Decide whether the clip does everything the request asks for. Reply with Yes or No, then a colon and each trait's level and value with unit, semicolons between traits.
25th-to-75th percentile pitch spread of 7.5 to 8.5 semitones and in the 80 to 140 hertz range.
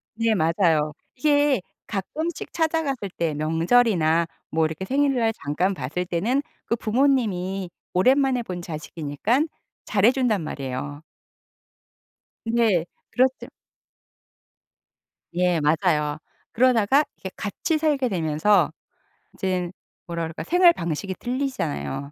No: wide, 7.8 semitones; high, 195 Hz